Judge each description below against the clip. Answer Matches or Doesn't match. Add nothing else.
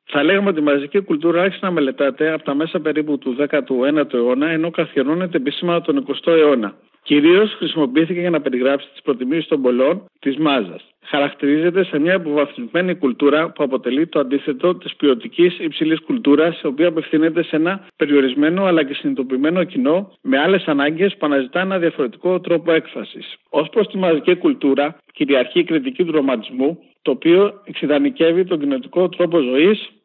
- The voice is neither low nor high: Matches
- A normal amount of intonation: Matches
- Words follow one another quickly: Doesn't match